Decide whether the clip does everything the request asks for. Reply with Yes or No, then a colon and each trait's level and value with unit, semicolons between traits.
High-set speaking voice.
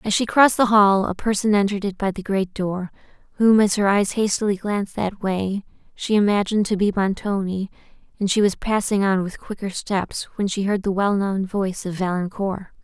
Yes: high, 200 Hz